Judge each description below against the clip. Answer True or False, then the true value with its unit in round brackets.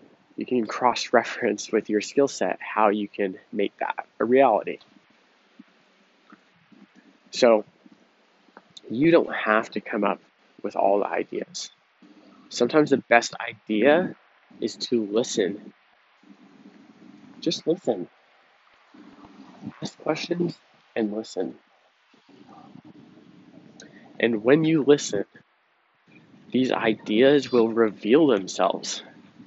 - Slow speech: True (100 wpm)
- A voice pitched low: True (120 Hz)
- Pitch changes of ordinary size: True (4.8 semitones)